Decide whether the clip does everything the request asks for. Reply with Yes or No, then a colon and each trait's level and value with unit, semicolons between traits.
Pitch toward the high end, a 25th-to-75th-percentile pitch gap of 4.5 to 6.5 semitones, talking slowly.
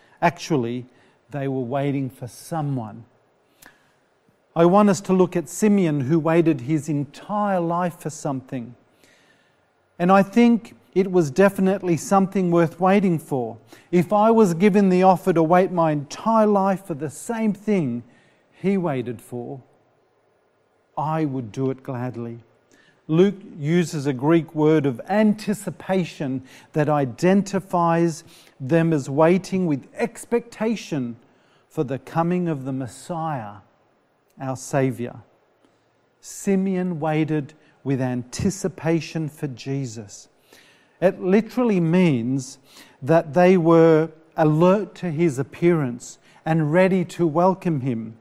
No: medium, 165 Hz; average, 5.3 semitones; slow, 120 wpm